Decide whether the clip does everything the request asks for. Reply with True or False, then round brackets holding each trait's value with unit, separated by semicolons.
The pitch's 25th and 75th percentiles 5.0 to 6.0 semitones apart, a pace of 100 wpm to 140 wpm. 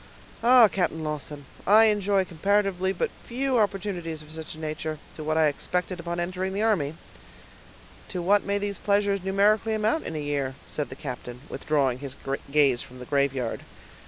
False (5.3 semitones; 170 wpm)